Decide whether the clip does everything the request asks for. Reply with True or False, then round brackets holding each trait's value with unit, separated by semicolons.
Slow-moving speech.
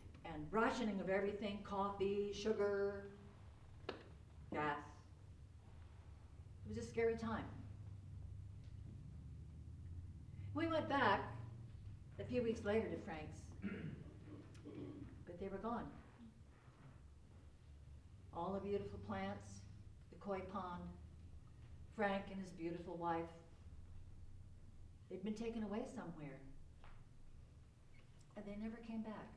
True (95 wpm)